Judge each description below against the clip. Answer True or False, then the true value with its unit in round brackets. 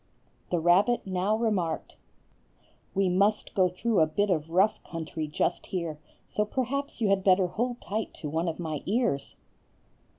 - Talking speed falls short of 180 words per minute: True (160 wpm)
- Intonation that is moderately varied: True (4.3 semitones)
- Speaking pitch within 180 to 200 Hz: True (185 Hz)